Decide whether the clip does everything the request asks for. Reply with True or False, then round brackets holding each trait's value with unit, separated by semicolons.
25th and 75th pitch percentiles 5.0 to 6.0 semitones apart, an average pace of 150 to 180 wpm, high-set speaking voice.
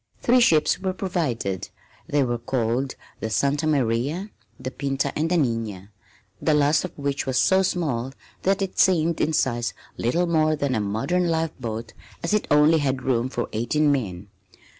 False (5.4 semitones; 170 wpm; 140 Hz)